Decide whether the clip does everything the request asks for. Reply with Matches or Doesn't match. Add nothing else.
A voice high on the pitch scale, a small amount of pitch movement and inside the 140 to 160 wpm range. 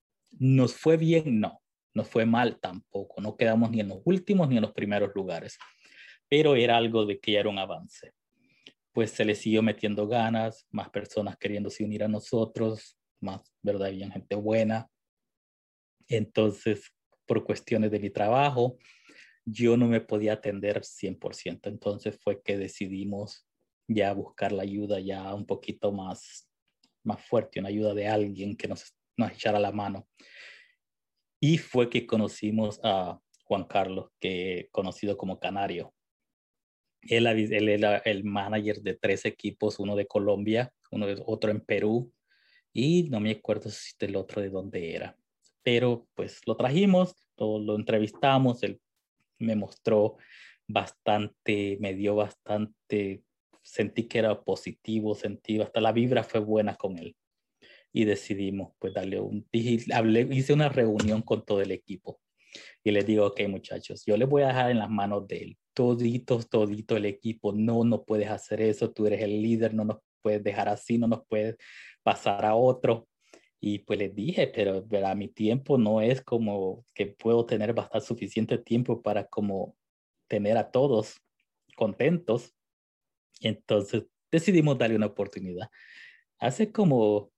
Doesn't match